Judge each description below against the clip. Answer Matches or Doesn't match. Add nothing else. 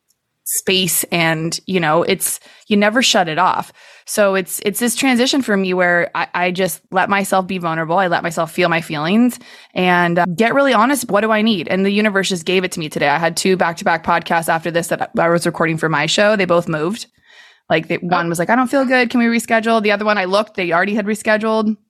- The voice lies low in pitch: Doesn't match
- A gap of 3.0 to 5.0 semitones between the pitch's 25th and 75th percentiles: Matches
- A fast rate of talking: Matches